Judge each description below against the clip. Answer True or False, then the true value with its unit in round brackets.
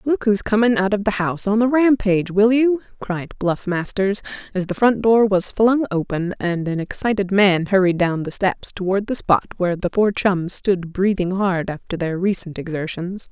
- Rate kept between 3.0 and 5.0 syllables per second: True (4.8 syllables/s)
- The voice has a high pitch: True (195 Hz)